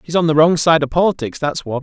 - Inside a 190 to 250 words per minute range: No, fast, 295 wpm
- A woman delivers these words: No, male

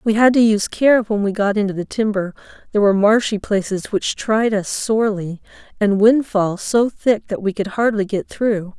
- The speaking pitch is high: Yes, high, 210 Hz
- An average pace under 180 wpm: No, average, 200 wpm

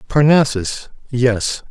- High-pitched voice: No, low, 130 Hz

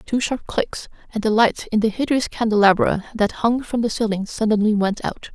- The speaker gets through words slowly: No, average, 200 wpm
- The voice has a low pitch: No, high, 220 Hz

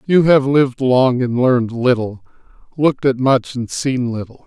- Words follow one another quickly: No, average, 175 wpm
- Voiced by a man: Yes, male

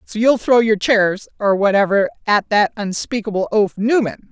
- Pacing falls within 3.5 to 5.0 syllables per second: Yes, 4.7 syllables/s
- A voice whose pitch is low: No, high, 210 Hz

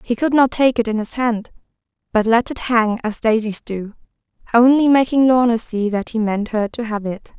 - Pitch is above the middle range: Yes, high, 230 Hz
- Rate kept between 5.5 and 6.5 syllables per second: No, 5.0 syllables/s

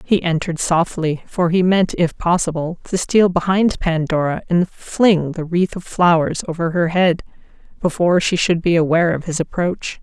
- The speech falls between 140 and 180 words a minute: Yes, average, 175 wpm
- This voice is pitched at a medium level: Yes, medium, 170 Hz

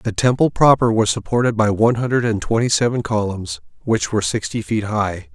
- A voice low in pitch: Yes, low, 115 Hz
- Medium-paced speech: Yes, average, 190 wpm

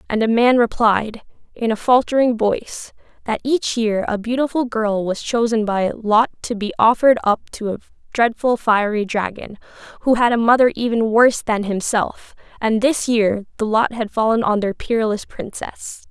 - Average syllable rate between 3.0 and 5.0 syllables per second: Yes, 4.8 syllables/s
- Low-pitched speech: No, high, 225 Hz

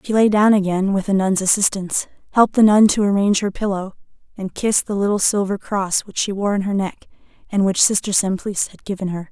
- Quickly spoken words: Yes, fast, 220 wpm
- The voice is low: No, high, 200 Hz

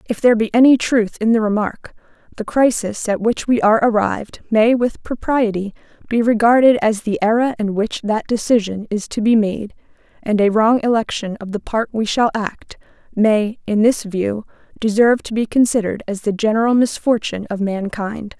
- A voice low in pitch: No, high, 220 Hz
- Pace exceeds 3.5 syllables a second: Yes, 5.2 syllables/s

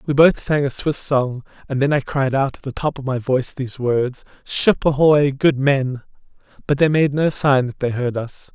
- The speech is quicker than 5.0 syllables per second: No, 4.8 syllables/s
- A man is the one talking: Yes, male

